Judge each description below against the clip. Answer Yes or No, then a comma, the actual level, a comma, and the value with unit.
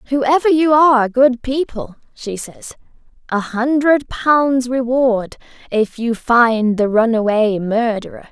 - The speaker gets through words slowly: Yes, slow, 125 wpm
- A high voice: Yes, high, 245 Hz